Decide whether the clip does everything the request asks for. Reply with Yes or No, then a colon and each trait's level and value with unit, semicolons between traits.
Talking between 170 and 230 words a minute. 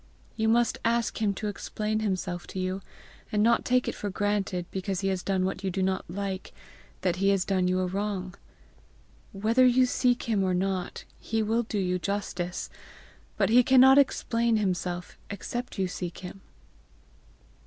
Yes: average, 175 wpm